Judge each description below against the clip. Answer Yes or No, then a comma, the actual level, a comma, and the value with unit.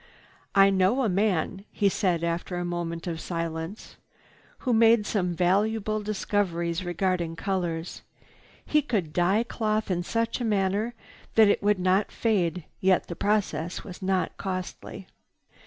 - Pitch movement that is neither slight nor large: Yes, average, 3.4 semitones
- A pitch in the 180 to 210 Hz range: Yes, high, 190 Hz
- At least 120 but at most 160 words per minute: Yes, average, 140 wpm